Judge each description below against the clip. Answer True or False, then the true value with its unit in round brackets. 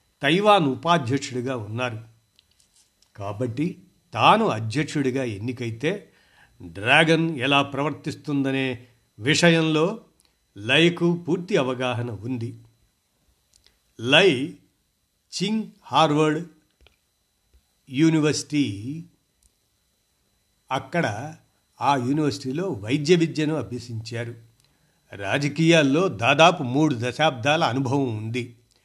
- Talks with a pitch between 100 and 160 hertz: True (140 Hz)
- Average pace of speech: False (65 wpm)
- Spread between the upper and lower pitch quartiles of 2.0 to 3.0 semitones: False (4.7 semitones)